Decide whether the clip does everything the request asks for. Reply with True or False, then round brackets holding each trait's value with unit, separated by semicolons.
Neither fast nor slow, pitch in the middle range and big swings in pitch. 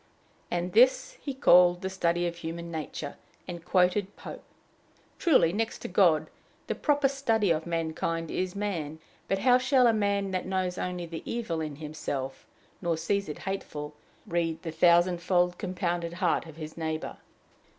False (160 wpm; 175 Hz; 3.3 semitones)